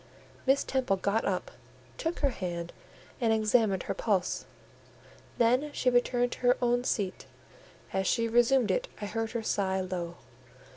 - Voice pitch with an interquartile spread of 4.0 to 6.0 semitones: Yes, average, 4.3 semitones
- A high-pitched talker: Yes, high, 225 Hz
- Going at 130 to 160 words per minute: Yes, average, 150 wpm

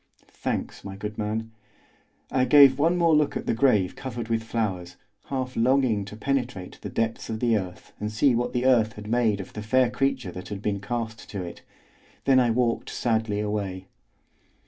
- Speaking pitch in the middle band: No, low, 115 Hz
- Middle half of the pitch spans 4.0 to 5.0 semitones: No, average, 3.4 semitones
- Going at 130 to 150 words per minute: No, average, 190 wpm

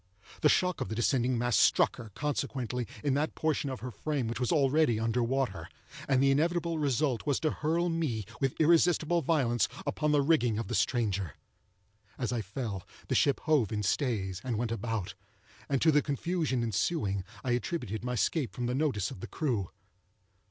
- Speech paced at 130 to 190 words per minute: Yes, average, 185 wpm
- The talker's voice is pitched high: No, low, 130 Hz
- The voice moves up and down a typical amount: Yes, average, 4.9 semitones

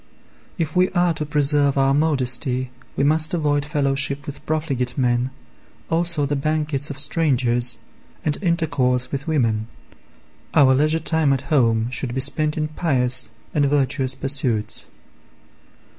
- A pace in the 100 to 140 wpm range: Yes, slow, 135 wpm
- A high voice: No, medium, 140 Hz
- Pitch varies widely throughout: No, average, 3.0 semitones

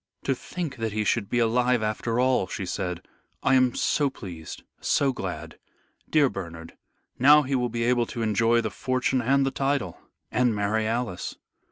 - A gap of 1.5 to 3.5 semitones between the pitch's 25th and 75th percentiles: No, average, 4.0 semitones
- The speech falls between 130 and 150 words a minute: No, average, 175 wpm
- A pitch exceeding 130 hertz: No, low, 120 Hz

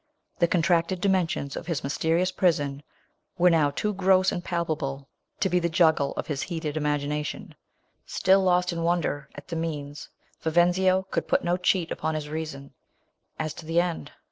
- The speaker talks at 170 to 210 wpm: Yes, average, 175 wpm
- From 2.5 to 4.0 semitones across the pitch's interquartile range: Yes, average, 3.2 semitones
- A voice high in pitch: No, medium, 165 Hz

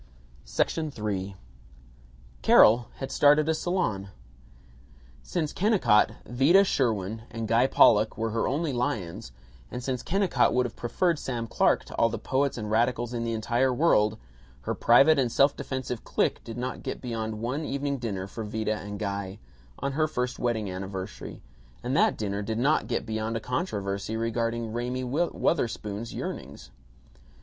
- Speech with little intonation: No, average, 3.8 semitones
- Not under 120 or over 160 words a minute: Yes, average, 155 wpm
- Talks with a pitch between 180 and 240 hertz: No, low, 115 Hz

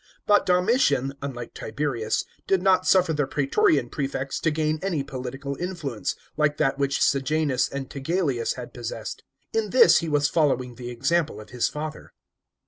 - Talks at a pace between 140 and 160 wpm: Yes, average, 155 wpm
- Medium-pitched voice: Yes, medium, 145 Hz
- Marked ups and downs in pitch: No, average, 3.8 semitones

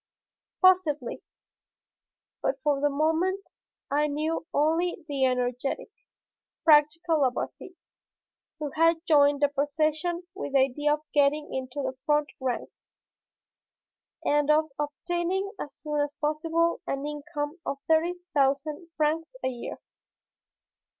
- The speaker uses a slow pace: Yes, slow, 115 wpm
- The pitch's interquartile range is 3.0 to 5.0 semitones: No, narrow, 2.4 semitones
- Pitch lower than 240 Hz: No, very high, 300 Hz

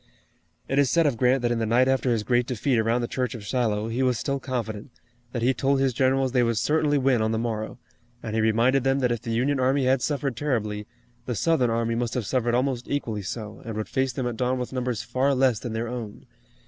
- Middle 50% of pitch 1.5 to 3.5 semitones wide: Yes, narrow, 2.6 semitones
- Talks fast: Yes, fast, 245 wpm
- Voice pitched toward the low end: Yes, low, 125 Hz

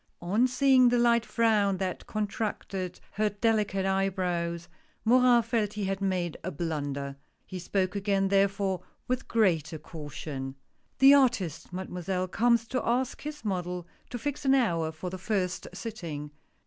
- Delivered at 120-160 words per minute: Yes, average, 150 wpm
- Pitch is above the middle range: Yes, high, 195 Hz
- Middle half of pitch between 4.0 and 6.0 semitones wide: Yes, average, 4.6 semitones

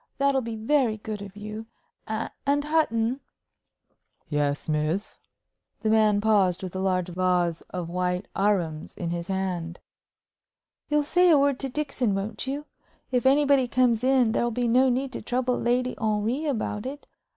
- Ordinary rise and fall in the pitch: No, wide, 5.7 semitones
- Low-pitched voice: No, high, 220 Hz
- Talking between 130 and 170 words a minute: Yes, average, 160 wpm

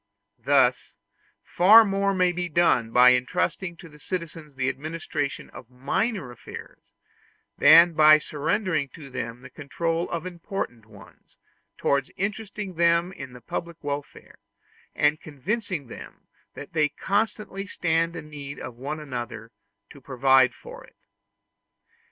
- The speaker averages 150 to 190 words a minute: No, average, 140 wpm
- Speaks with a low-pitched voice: No, medium, 155 Hz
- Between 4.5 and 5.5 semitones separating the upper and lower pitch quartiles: Yes, average, 4.8 semitones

